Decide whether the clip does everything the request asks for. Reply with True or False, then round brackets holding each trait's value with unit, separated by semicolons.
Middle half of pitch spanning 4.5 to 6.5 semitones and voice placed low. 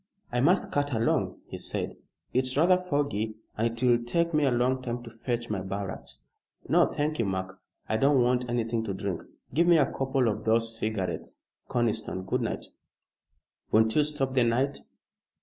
False (3.7 semitones; 120 Hz)